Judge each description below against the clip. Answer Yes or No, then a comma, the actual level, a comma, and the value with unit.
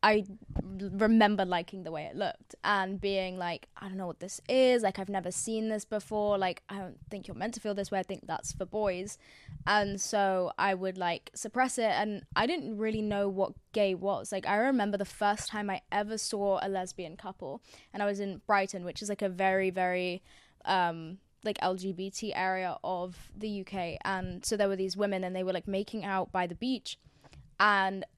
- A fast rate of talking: Yes, fast, 210 wpm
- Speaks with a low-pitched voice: No, high, 195 Hz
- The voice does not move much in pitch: Yes, narrow, 2.0 semitones